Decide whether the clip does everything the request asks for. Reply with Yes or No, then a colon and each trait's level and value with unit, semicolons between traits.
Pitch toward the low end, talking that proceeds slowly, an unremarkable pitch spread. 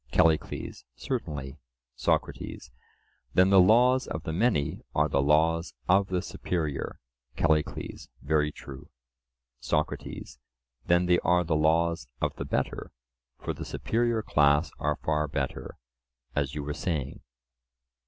Yes: very low, 80 Hz; slow, 125 wpm; average, 3.4 semitones